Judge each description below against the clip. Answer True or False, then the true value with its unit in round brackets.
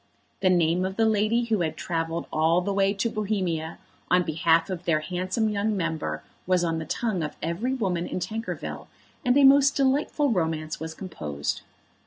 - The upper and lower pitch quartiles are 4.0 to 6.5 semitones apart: True (4.9 semitones)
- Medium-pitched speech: True (180 Hz)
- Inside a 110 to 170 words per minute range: False (180 wpm)